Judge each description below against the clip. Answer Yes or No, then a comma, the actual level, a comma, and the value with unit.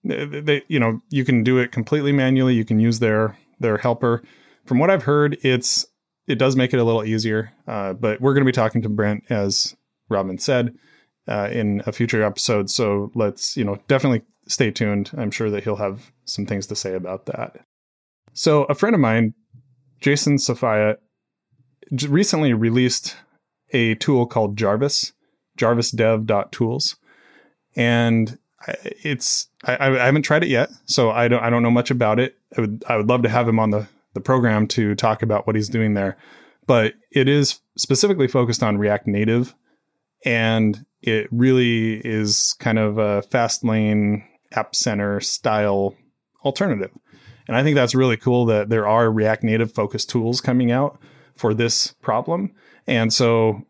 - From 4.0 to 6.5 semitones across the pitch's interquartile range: No, average, 3.3 semitones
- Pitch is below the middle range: Yes, low, 115 Hz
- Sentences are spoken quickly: No, average, 170 wpm